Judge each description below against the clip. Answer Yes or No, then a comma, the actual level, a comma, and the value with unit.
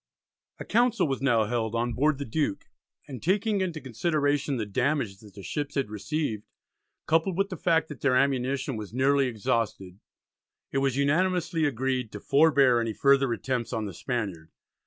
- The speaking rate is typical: Yes, average, 170 wpm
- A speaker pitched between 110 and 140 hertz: Yes, low, 135 Hz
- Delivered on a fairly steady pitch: No, average, 4.9 semitones